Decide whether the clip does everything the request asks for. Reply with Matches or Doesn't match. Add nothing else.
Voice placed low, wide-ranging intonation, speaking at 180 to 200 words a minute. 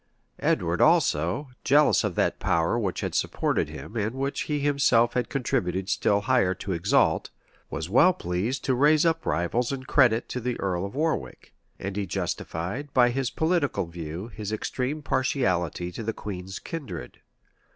Doesn't match